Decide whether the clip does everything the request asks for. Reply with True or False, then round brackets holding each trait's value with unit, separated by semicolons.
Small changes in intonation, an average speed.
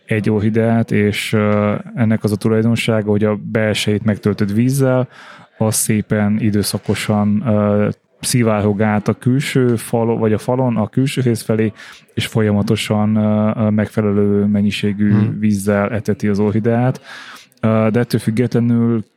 True (1.6 semitones; 115 wpm)